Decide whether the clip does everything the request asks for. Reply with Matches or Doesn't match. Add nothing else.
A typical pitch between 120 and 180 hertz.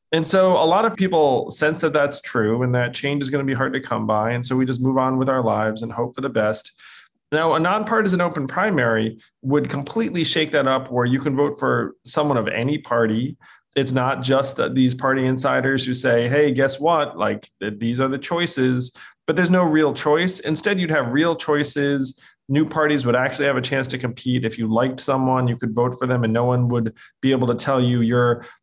Matches